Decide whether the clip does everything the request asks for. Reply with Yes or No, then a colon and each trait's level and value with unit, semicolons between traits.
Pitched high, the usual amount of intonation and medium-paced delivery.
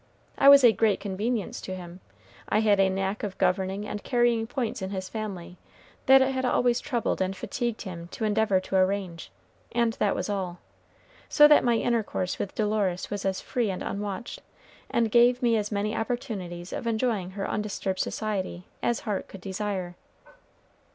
Yes: high, 205 Hz; average, 3.6 semitones; average, 175 wpm